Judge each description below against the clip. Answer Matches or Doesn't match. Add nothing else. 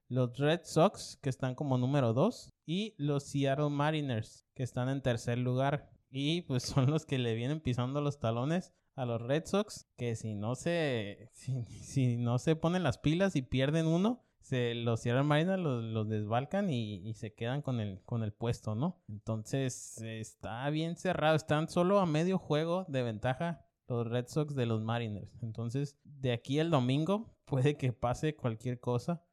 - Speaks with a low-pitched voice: Matches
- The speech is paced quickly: Doesn't match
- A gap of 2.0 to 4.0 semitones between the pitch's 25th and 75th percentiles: Doesn't match